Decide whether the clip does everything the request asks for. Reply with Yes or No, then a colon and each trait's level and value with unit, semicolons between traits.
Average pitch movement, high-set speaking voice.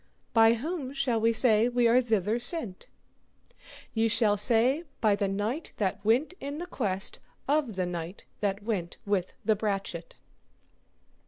Yes: average, 3.8 semitones; high, 225 Hz